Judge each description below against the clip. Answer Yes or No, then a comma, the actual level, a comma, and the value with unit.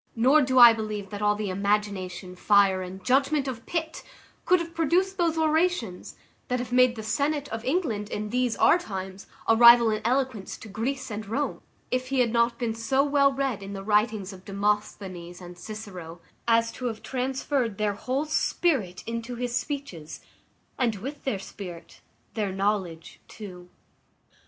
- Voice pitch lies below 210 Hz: No, high, 225 Hz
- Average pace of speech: Yes, average, 170 wpm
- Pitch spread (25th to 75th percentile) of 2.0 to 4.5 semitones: No, average, 4.9 semitones